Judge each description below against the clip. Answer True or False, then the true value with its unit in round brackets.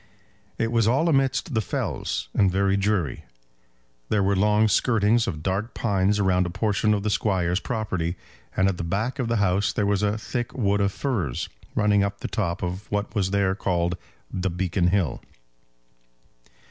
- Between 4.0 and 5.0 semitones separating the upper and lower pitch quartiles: False (2.5 semitones)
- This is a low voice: True (100 Hz)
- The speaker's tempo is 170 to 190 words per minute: True (180 wpm)